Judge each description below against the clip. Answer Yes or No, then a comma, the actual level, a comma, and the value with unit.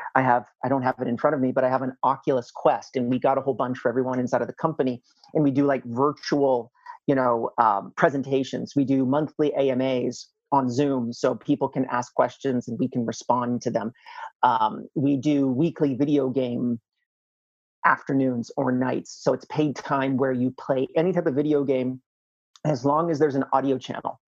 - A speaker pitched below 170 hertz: Yes, low, 135 Hz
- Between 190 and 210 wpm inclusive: Yes, fast, 205 wpm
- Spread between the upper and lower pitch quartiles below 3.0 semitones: Yes, narrow, 2.4 semitones